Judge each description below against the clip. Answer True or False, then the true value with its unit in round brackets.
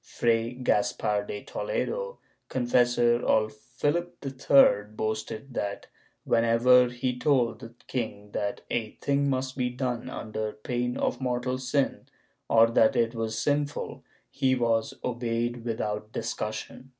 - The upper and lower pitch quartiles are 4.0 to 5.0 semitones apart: False (2.6 semitones)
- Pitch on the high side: False (120 Hz)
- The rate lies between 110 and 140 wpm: True (135 wpm)